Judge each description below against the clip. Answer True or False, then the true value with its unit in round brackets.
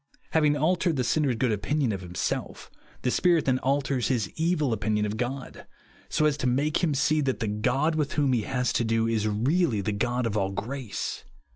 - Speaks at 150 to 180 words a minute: False (205 wpm)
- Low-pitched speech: True (130 Hz)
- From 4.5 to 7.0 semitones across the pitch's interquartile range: True (5.2 semitones)